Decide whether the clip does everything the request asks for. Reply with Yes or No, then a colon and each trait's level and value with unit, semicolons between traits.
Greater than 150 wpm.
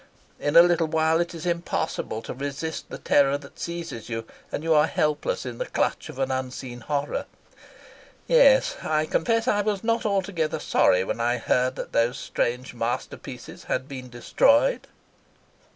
Yes: average, 165 wpm